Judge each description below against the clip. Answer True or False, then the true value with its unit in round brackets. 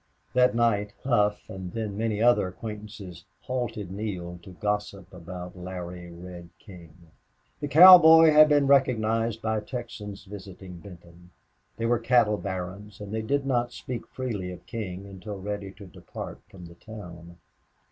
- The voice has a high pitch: False (105 Hz)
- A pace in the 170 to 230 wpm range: False (145 wpm)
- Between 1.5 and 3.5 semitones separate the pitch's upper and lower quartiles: False (4.2 semitones)